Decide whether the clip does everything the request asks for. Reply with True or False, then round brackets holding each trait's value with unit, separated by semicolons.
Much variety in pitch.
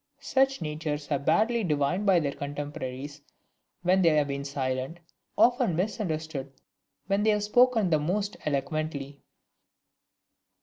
True (6.1 semitones)